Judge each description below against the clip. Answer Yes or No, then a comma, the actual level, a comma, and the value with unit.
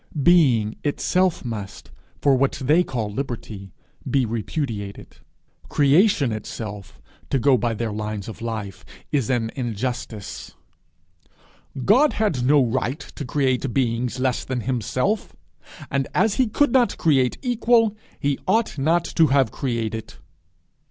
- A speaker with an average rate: No, slow, 130 wpm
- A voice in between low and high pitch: No, low, 130 Hz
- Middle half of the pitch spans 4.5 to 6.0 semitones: Yes, average, 4.9 semitones